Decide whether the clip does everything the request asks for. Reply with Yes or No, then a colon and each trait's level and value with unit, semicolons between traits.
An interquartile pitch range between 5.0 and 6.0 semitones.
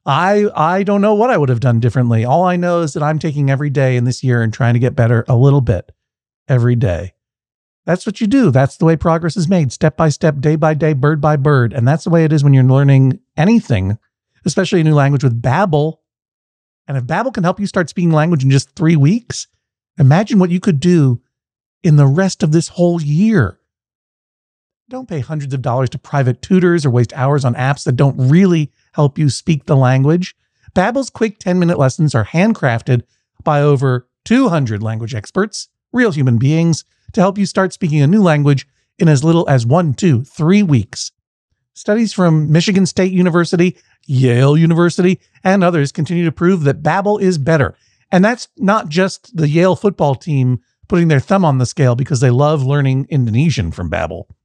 Yes: wide, 5.5 semitones